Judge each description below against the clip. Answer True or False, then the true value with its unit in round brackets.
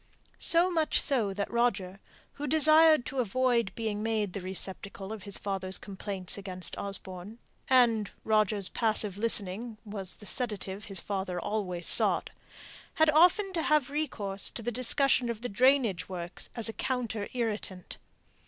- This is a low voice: False (215 Hz)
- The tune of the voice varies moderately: True (4.6 semitones)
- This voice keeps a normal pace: True (150 wpm)